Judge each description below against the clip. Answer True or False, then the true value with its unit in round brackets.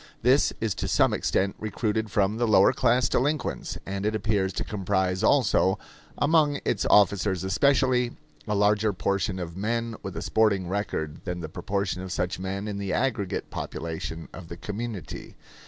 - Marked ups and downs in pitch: False (3.1 semitones)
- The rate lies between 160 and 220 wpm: True (165 wpm)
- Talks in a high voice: False (100 Hz)